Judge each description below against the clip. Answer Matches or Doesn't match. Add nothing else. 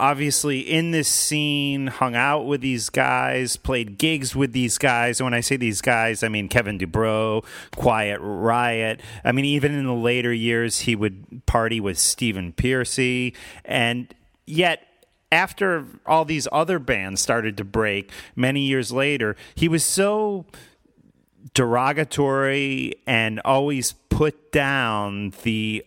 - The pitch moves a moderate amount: Matches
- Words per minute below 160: Matches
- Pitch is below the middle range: Matches